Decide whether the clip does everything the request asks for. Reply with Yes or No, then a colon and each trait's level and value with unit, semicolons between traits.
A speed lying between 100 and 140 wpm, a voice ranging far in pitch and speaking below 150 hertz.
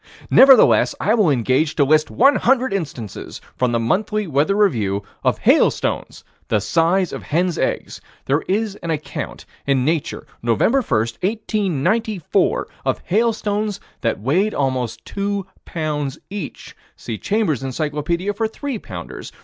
No: slow, 135 wpm; wide, 7.6 semitones; medium, 165 Hz